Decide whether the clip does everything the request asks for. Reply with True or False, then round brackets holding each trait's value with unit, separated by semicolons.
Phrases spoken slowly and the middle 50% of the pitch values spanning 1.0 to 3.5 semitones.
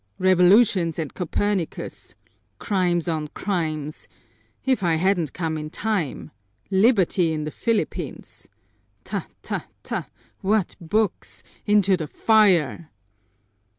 False (105 wpm; 4.2 semitones)